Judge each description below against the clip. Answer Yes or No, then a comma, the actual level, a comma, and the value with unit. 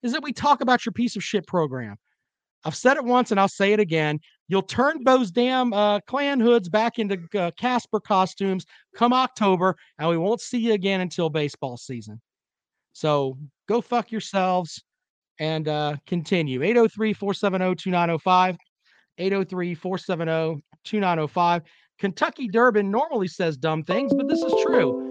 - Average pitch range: No, wide, 5.9 semitones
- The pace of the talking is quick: No, average, 155 wpm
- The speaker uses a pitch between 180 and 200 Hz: Yes, high, 190 Hz